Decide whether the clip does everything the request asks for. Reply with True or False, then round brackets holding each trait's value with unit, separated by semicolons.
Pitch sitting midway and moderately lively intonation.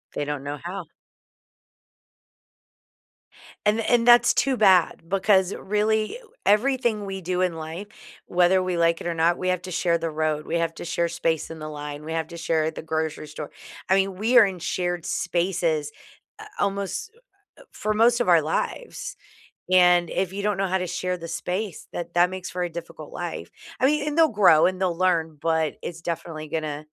True (180 Hz; 3.4 semitones)